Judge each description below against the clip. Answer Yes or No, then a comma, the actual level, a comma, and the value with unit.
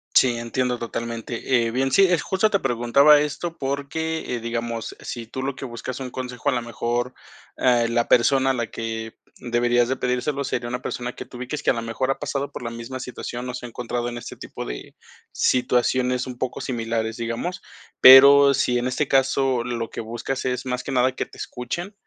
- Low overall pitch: Yes, low, 125 Hz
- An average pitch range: No, narrow, 2.2 semitones